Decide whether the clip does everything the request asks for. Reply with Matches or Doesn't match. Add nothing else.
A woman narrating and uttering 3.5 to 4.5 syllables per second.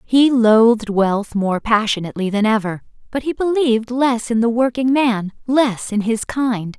Matches